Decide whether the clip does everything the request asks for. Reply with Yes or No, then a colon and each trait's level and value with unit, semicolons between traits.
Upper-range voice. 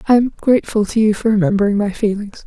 Yes: high, 215 Hz